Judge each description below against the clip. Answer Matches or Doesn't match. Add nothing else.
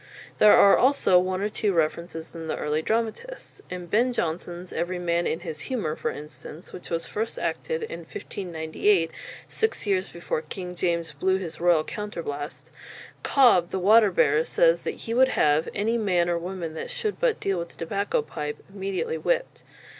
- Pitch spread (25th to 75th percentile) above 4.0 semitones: Matches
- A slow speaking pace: Doesn't match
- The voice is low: Doesn't match